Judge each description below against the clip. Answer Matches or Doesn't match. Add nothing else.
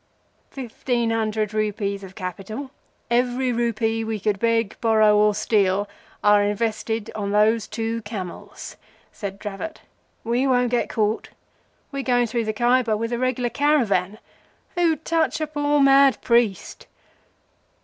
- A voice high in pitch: Matches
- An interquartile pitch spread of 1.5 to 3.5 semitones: Matches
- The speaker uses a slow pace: Matches